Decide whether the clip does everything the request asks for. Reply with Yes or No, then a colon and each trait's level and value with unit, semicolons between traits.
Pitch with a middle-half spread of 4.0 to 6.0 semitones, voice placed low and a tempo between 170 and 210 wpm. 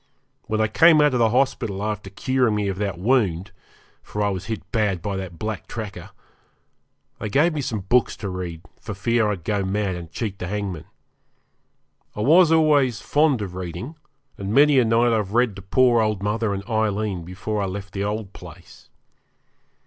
No: average, 3.6 semitones; low, 105 Hz; average, 185 wpm